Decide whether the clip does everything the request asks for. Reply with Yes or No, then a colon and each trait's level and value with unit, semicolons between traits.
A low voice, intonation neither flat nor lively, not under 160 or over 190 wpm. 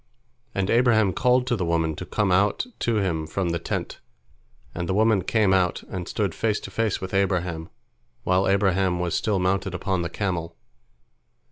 Yes: very low, 95 Hz; average, 3.0 semitones; average, 175 wpm